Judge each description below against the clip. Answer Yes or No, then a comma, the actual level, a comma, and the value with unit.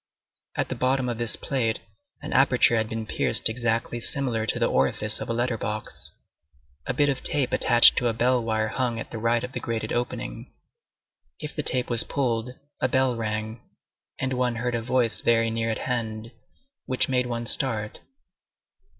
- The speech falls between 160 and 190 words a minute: Yes, average, 185 wpm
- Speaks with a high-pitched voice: No, low, 120 Hz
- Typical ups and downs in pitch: No, narrow, 2.1 semitones